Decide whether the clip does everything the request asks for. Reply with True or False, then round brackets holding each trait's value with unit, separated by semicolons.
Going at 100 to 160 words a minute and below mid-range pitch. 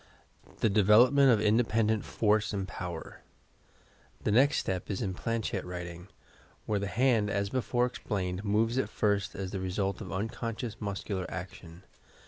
True (145 wpm; 105 Hz)